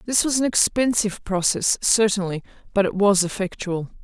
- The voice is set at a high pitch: Yes, high, 205 Hz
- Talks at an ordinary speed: Yes, average, 150 wpm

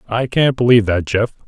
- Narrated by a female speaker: No, male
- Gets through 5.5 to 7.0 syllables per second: Yes, 6.0 syllables/s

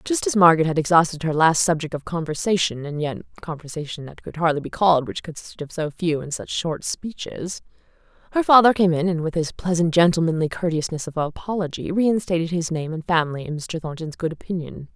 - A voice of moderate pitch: Yes, medium, 165 Hz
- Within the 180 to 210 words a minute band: Yes, average, 190 wpm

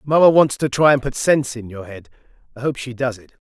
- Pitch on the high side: No, low, 130 Hz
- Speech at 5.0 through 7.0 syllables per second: Yes, 5.7 syllables/s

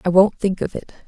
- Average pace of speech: No, fast, 280 wpm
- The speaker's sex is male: No, female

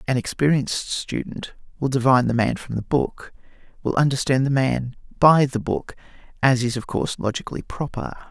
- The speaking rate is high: No, average, 165 wpm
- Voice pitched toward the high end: No, low, 130 Hz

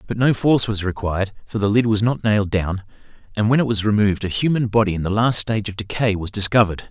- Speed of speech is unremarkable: No, fast, 245 wpm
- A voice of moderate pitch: No, low, 105 Hz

